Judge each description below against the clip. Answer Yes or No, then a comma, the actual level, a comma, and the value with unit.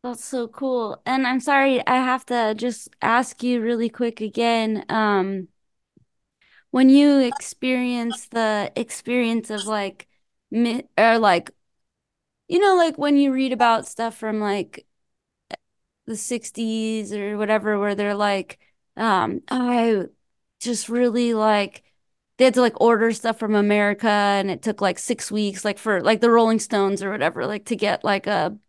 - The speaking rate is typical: Yes, average, 155 wpm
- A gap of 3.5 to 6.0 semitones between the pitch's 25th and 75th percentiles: No, average, 2.8 semitones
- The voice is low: No, high, 230 Hz